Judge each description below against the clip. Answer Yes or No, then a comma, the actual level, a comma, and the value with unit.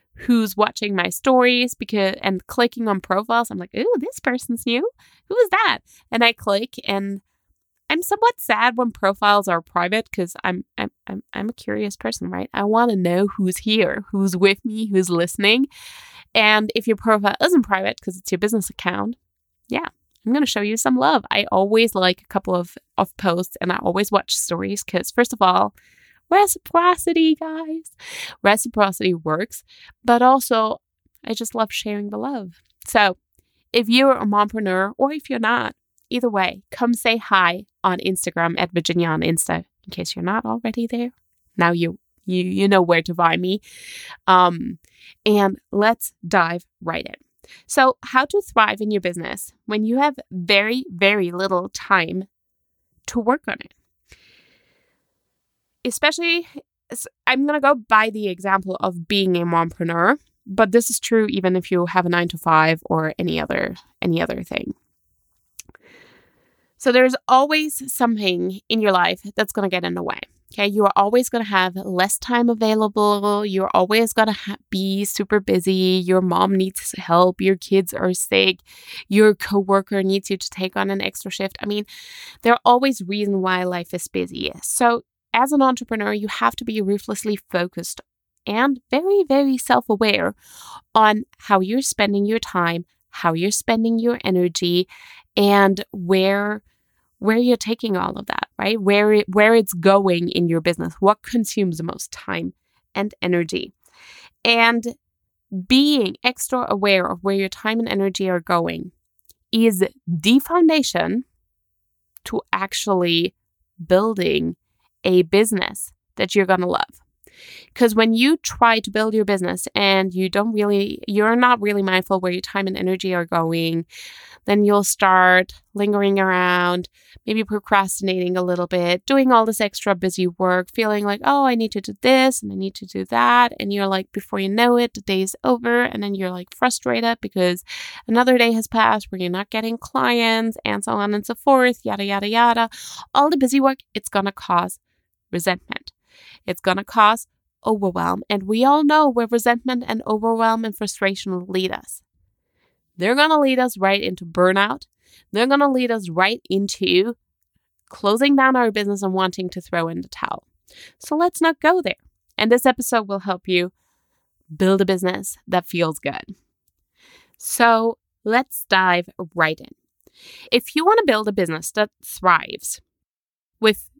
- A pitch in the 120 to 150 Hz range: No, high, 205 Hz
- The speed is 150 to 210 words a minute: Yes, average, 170 wpm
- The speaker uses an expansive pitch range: No, average, 4.3 semitones